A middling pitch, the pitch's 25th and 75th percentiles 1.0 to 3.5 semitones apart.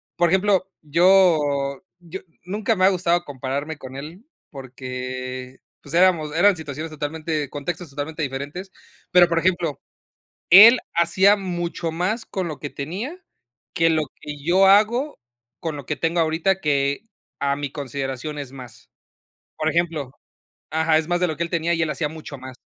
No: medium, 160 Hz; average, 4.1 semitones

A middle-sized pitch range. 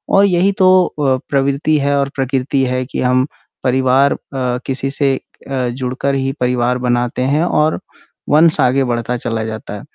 No: narrow, 2.0 semitones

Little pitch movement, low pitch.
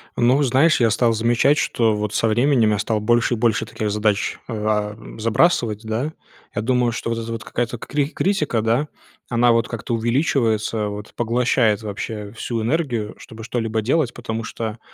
Yes: narrow, 2.2 semitones; low, 115 Hz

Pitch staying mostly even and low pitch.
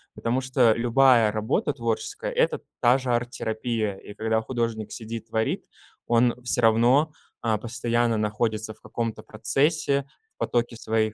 Yes: narrow, 2.2 semitones; low, 115 Hz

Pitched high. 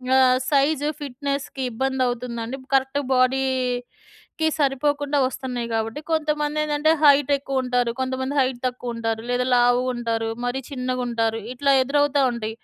Yes: very high, 260 Hz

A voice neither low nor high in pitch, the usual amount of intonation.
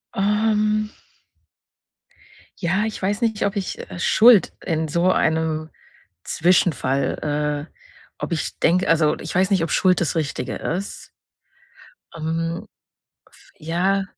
Yes: medium, 175 Hz; average, 3.8 semitones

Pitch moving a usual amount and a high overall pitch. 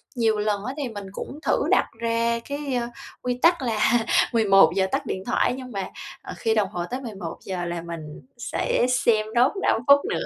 Yes: average, 4.3 semitones; high, 225 Hz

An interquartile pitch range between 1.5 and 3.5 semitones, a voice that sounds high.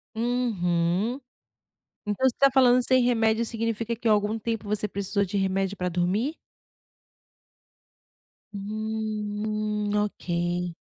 Yes: average, 2.7 semitones; high, 210 Hz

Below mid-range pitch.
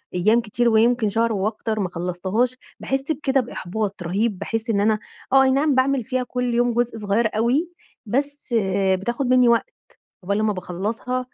No: high, 230 Hz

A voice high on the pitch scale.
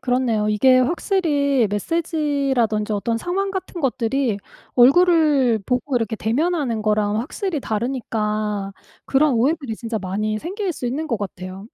Yes: very high, 250 Hz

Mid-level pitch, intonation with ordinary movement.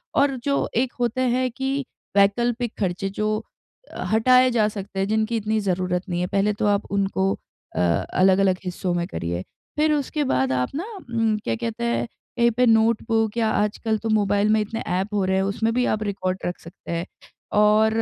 No: high, 215 Hz; average, 3.5 semitones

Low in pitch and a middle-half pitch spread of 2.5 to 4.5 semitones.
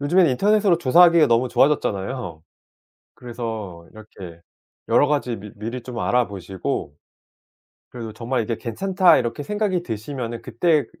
No: low, 125 Hz; wide, 5.5 semitones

